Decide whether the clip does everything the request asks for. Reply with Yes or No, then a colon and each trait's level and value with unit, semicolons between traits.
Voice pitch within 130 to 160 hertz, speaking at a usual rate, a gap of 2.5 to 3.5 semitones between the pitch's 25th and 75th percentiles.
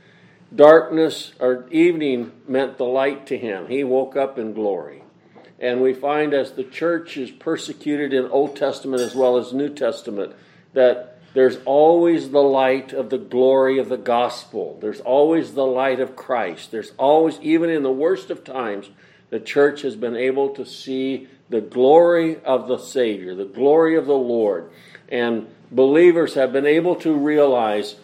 Yes: low, 135 Hz; average, 165 wpm; average, 2.8 semitones